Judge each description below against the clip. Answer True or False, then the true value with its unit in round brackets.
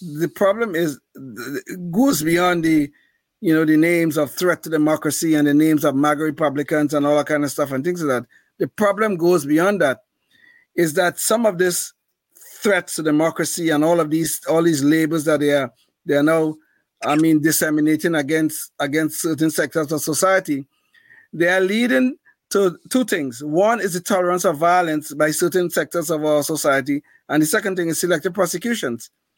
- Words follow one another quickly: False (185 wpm)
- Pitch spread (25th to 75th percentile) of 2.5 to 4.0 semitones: True (2.9 semitones)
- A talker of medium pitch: True (160 Hz)